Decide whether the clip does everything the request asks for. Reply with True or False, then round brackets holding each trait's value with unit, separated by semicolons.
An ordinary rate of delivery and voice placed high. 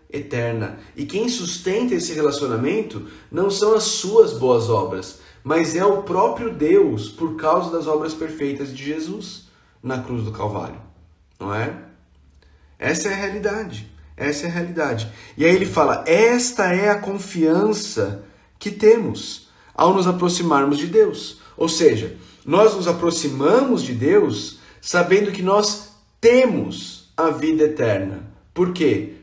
False (140 wpm; 160 Hz)